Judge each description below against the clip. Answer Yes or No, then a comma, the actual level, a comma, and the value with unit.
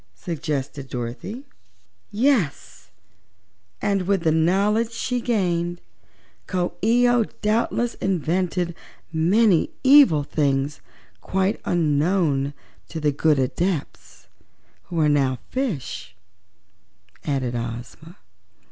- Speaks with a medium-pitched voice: Yes, medium, 170 Hz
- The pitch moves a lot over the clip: Yes, wide, 6.1 semitones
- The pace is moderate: No, slow, 95 wpm